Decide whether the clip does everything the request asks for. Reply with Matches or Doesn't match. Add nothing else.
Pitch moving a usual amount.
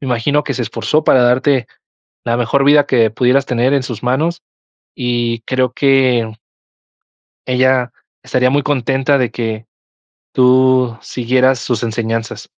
Doesn't match